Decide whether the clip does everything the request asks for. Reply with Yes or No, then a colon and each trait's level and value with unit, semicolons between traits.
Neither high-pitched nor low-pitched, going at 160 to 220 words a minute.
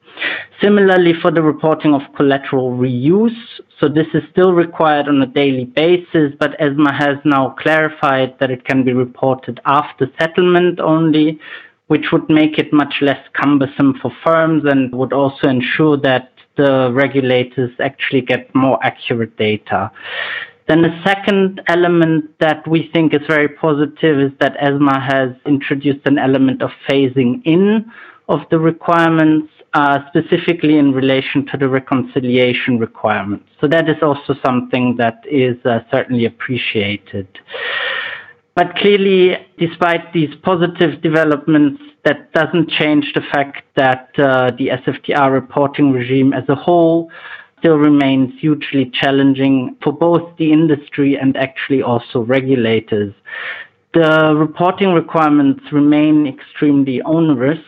No: medium, 145 Hz; slow, 135 wpm